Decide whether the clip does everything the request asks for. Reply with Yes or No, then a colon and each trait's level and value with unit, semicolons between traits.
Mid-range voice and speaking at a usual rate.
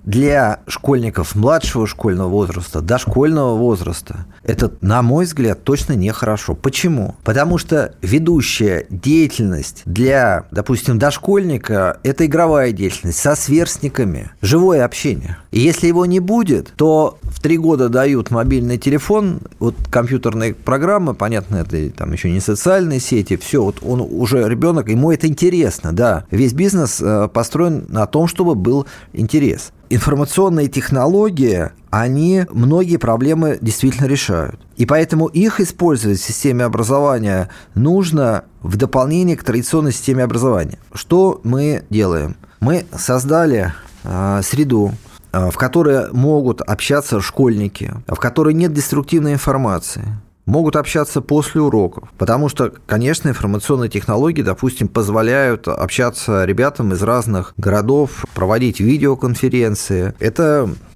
No: low, 125 Hz; average, 125 wpm